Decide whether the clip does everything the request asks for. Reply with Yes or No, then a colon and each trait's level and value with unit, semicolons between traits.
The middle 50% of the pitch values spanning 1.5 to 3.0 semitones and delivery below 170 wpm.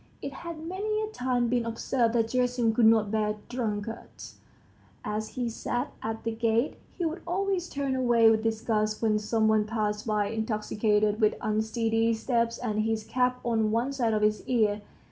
No: narrow, 2.5 semitones; average, 175 wpm